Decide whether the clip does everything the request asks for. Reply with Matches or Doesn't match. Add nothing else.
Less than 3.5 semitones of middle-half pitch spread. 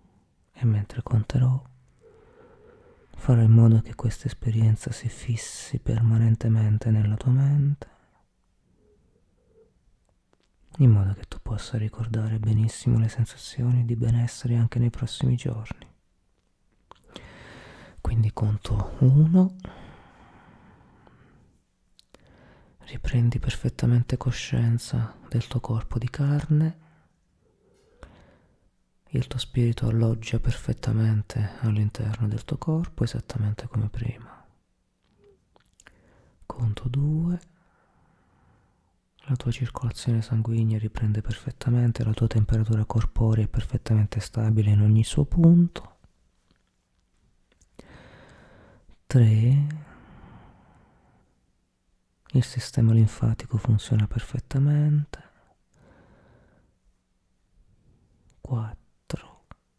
Matches